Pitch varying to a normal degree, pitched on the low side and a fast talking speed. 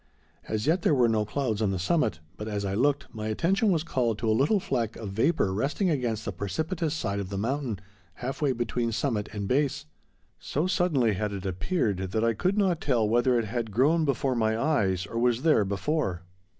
No: wide, 5.8 semitones; low, 115 Hz; fast, 210 wpm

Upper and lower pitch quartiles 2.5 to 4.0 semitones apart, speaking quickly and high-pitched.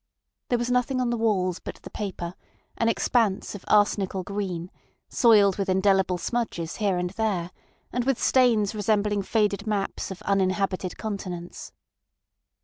No: average, 3.1 semitones; average, 145 wpm; high, 200 Hz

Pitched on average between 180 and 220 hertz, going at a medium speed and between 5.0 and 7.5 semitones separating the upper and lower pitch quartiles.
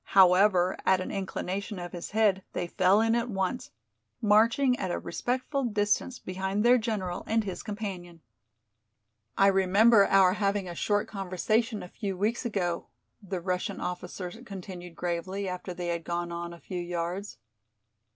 No: high, 190 Hz; average, 155 wpm; average, 3.0 semitones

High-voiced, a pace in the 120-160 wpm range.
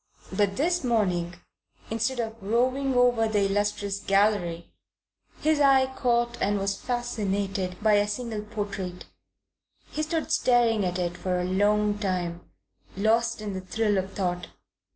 Yes: high, 210 Hz; average, 140 wpm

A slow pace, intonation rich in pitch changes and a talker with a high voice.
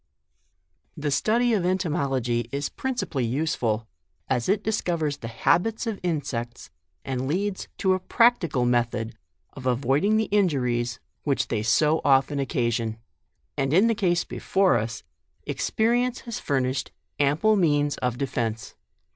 No: slow, 130 wpm; wide, 7.5 semitones; medium, 145 Hz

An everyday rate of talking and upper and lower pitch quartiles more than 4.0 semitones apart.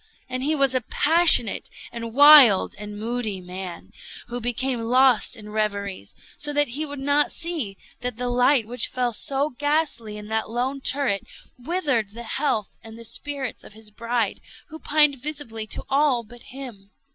Yes: average, 170 wpm; average, 4.4 semitones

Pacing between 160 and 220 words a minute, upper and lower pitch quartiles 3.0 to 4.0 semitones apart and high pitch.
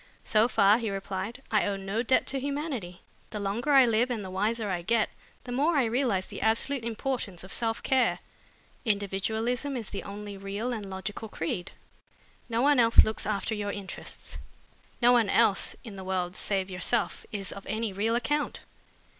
Yes: average, 180 wpm; average, 3.6 semitones; high, 220 Hz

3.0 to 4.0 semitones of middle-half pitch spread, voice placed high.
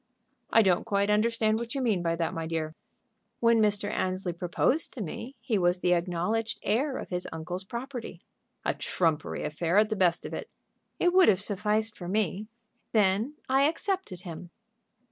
No: average, 4.5 semitones; high, 205 Hz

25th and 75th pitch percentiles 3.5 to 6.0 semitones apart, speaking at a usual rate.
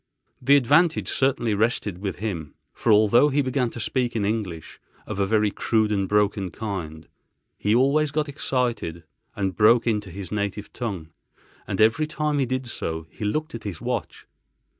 Yes: average, 4.6 semitones; average, 165 wpm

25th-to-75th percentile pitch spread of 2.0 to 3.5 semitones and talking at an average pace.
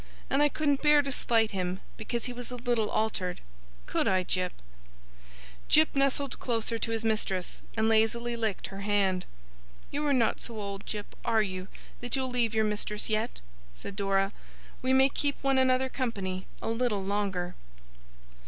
No: average, 4.3 semitones; average, 170 wpm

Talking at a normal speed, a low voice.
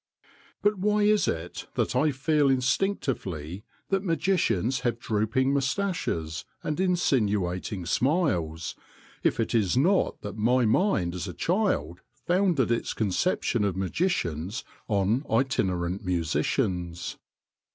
No: slow, 115 wpm; low, 115 Hz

